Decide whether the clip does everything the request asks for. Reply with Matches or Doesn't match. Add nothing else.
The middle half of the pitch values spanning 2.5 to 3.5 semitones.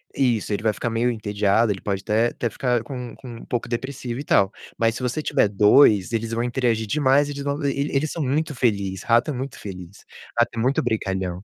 Doesn't match